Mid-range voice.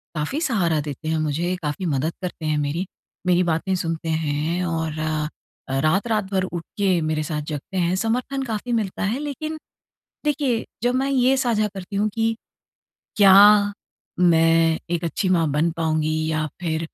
Yes: medium, 175 Hz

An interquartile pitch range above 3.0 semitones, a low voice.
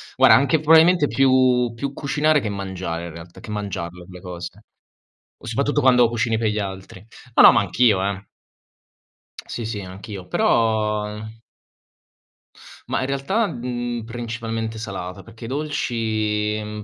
Yes: average, 4.0 semitones; low, 110 Hz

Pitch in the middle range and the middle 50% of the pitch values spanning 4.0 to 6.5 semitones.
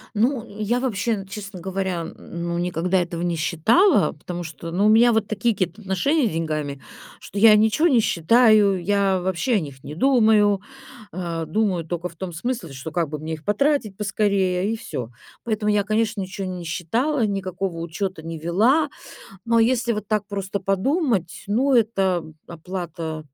No: high, 195 Hz; average, 4.4 semitones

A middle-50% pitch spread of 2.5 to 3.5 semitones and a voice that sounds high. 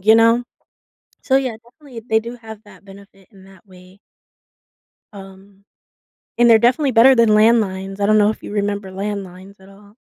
Yes: average, 2.9 semitones; high, 205 Hz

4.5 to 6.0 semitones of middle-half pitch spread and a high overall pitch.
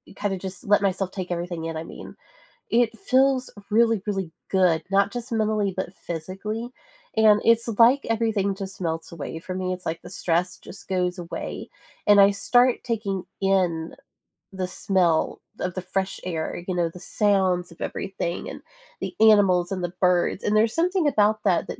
No: average, 3.3 semitones; high, 195 Hz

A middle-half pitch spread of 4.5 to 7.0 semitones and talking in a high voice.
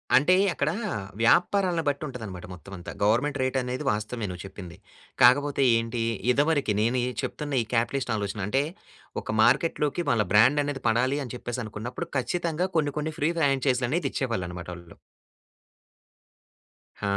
No: average, 4.9 semitones; low, 130 Hz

